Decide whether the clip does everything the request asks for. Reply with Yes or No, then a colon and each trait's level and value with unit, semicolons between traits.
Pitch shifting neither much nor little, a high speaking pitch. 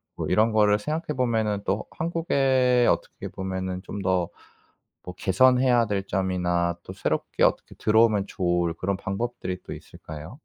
No: average, 4.7 semitones; low, 100 Hz